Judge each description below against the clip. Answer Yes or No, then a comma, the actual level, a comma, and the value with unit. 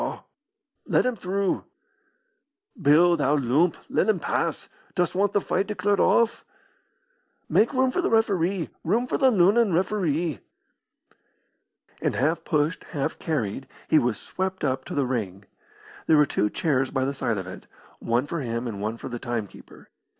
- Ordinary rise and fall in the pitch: No, wide, 7.2 semitones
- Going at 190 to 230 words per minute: No, average, 160 wpm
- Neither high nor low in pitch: Yes, medium, 160 Hz